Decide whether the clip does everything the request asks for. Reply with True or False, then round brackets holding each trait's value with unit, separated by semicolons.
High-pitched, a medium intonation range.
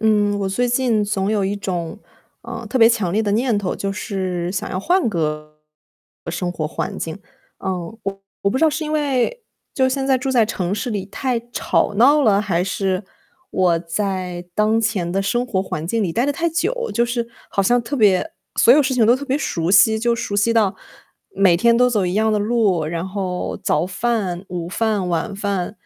True (205 Hz; 4.4 semitones)